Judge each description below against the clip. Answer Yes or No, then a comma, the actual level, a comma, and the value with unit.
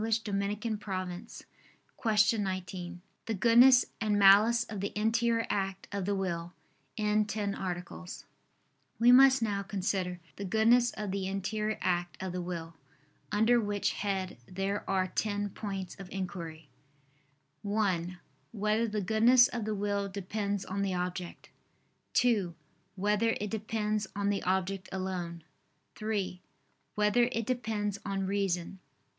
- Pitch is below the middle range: No, high, 200 Hz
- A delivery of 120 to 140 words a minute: Yes, slow, 135 wpm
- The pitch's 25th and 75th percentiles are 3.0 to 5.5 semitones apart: No, narrow, 2.5 semitones